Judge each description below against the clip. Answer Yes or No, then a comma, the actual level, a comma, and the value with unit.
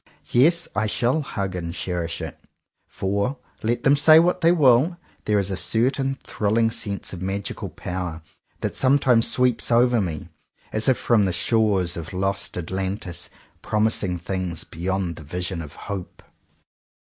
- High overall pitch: No, low, 100 Hz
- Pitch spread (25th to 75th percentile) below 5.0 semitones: No, wide, 5.4 semitones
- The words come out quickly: No, average, 150 wpm